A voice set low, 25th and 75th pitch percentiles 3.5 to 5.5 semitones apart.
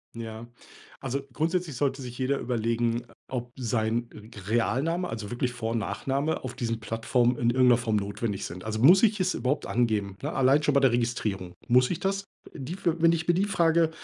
Yes: low, 125 Hz; average, 4.5 semitones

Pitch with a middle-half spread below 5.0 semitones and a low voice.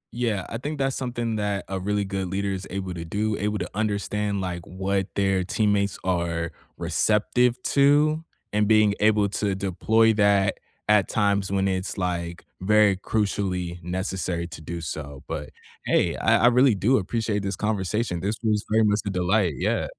Yes: narrow, 2.5 semitones; low, 100 Hz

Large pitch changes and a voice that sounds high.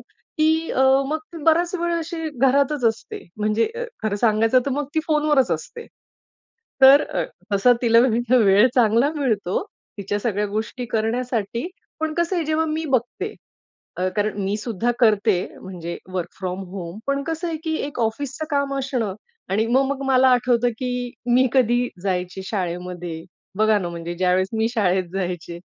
Yes: wide, 5.9 semitones; high, 235 Hz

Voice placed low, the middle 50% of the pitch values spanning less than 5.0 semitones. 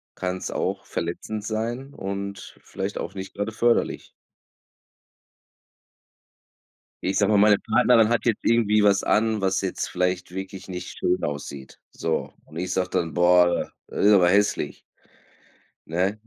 Yes: low, 100 Hz; average, 2.9 semitones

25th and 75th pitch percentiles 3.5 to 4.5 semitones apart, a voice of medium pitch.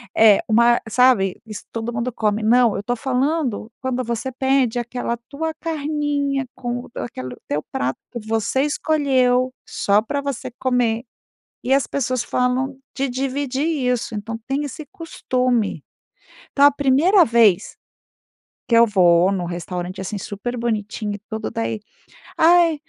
No: average, 3.8 semitones; high, 245 Hz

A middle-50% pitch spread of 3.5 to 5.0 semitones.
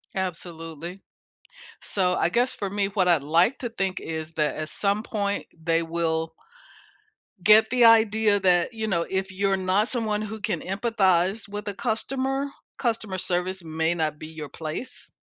Yes: average, 4.4 semitones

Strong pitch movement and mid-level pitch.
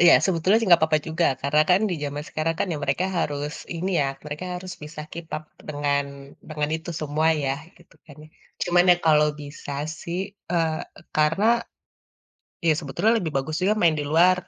No: average, 2.7 semitones; medium, 155 Hz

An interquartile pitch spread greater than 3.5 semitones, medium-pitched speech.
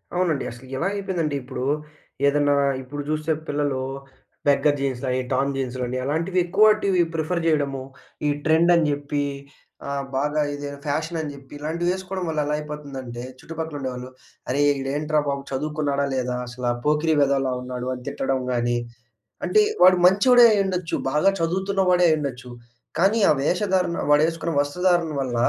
Yes: average, 4.1 semitones; medium, 150 Hz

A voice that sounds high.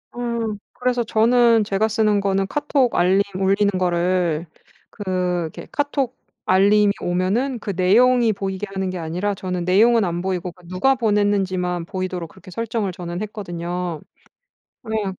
Yes: high, 195 Hz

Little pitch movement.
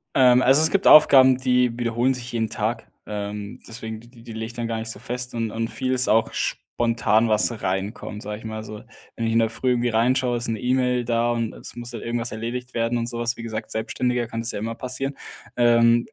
Yes: narrow, 1.8 semitones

